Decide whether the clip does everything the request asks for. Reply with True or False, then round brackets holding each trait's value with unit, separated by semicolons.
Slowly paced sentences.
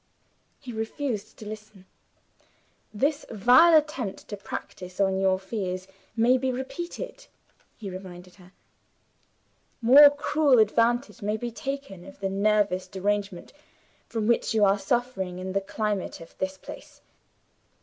True (130 wpm)